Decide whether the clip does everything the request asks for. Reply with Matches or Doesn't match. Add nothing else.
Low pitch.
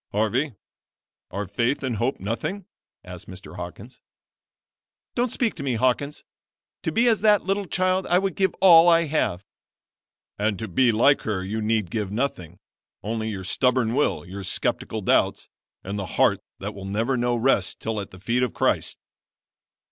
Matches